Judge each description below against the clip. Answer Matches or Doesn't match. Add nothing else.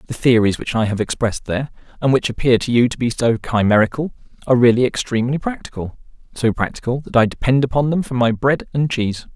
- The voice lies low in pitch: Matches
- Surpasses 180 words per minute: Matches